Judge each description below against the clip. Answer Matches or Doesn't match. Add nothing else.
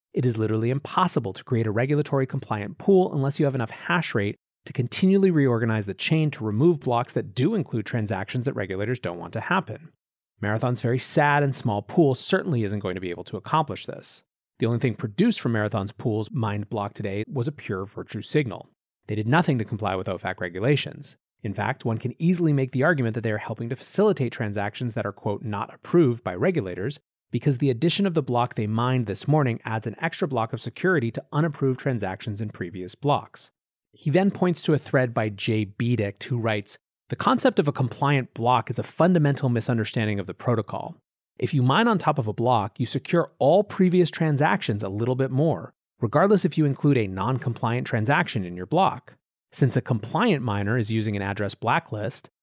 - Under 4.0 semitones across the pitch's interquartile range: Doesn't match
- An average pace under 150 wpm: Doesn't match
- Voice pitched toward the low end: Matches